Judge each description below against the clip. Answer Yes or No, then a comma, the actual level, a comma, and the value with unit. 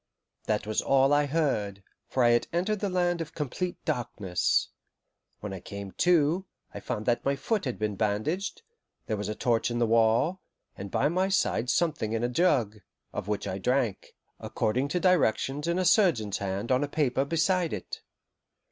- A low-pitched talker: Yes, low, 130 Hz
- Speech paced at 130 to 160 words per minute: No, average, 185 wpm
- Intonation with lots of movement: Yes, wide, 7.7 semitones